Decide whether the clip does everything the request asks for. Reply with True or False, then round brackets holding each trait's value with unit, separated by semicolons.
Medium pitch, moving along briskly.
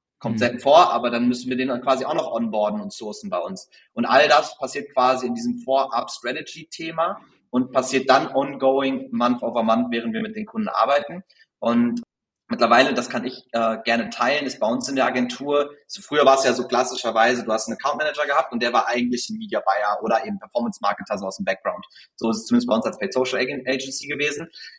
False (130 Hz; 210 wpm)